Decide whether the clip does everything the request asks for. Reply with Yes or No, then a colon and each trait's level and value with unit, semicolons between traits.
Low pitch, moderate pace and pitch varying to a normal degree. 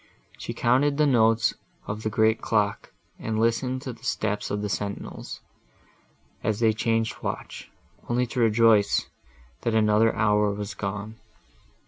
No: low, 110 Hz; average, 145 wpm; narrow, 1.9 semitones